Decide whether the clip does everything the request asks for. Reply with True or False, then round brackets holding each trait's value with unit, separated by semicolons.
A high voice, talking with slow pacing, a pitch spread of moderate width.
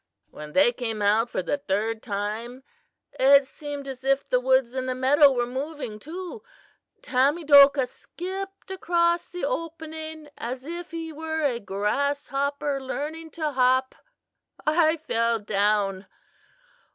True (275 Hz; 130 wpm; 4.8 semitones)